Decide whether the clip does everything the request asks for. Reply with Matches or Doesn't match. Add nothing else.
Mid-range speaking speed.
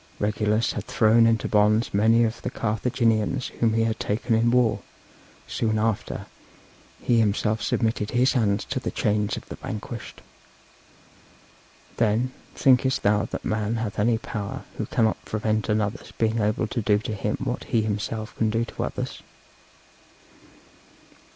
Matches